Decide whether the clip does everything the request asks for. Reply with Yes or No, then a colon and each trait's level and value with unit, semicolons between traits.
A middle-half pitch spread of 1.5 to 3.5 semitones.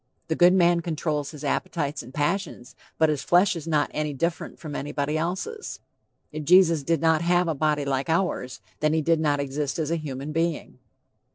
Yes: average, 2.7 semitones